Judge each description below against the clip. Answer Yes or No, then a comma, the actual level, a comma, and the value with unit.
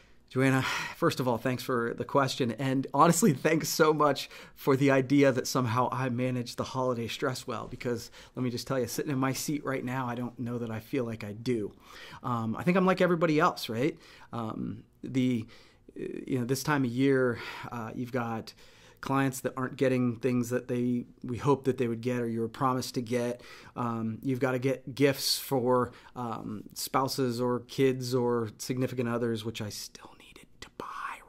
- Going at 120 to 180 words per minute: No, average, 190 wpm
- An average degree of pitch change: No, narrow, 1.9 semitones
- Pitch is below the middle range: Yes, low, 130 Hz